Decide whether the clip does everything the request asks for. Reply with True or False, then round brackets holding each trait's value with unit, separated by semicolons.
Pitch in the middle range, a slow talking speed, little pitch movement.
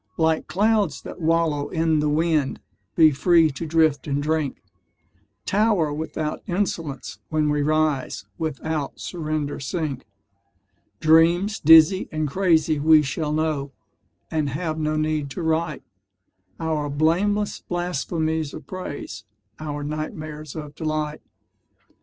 True (155 Hz; 120 wpm; 1.7 semitones)